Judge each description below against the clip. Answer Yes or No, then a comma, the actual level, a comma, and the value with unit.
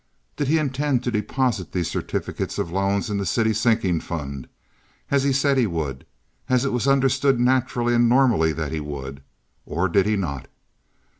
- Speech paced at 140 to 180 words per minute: Yes, average, 165 wpm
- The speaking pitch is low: Yes, low, 110 Hz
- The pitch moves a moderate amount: No, wide, 8.1 semitones